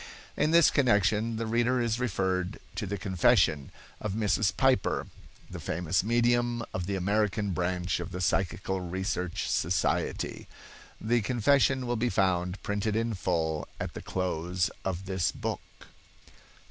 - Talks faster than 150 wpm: No, average, 140 wpm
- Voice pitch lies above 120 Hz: No, low, 100 Hz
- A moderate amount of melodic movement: Yes, average, 4.2 semitones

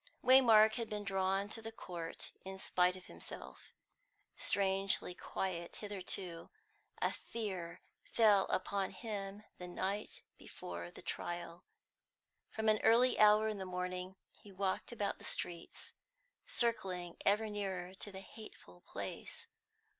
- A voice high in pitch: Yes, high, 195 Hz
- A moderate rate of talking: No, slow, 130 wpm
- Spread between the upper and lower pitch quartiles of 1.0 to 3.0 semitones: Yes, average, 2.7 semitones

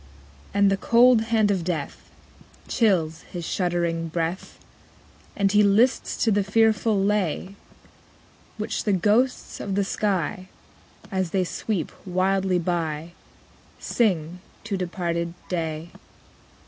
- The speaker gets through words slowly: Yes, slow, 120 wpm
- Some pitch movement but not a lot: Yes, average, 3.3 semitones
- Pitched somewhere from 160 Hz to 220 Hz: Yes, high, 190 Hz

